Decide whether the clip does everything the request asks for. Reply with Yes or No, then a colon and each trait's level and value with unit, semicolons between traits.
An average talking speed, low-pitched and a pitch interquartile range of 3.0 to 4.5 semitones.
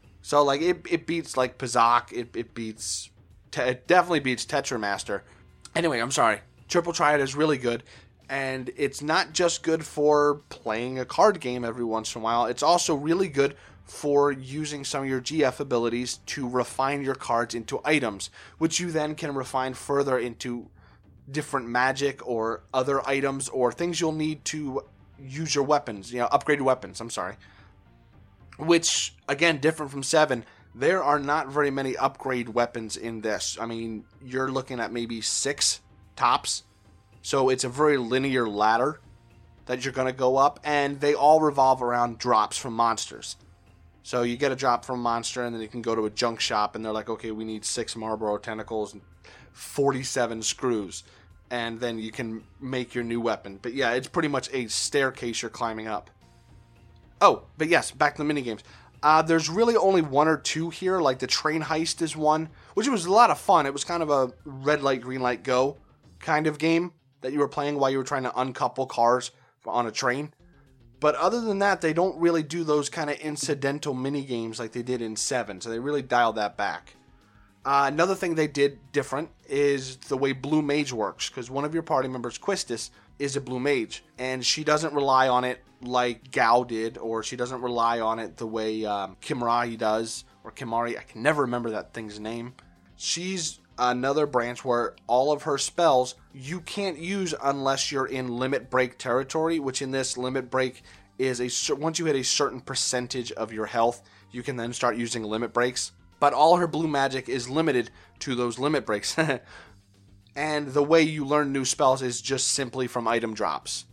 Yes: average, 190 wpm; low, 130 Hz; average, 4.0 semitones